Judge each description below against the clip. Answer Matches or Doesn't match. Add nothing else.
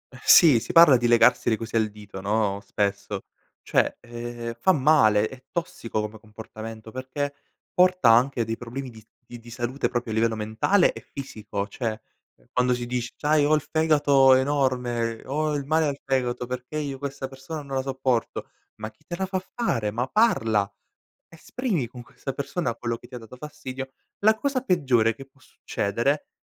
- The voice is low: Matches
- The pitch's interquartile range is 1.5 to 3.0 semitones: Doesn't match